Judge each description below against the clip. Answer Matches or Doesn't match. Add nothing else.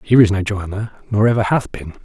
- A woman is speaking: Doesn't match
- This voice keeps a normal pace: Doesn't match